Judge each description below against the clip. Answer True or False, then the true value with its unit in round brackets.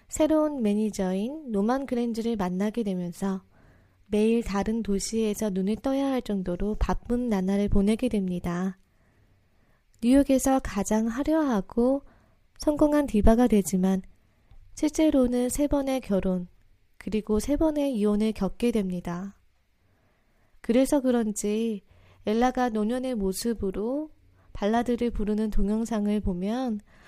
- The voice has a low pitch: False (215 Hz)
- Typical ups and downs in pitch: True (4.5 semitones)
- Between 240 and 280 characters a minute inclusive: True (260 characters per minute)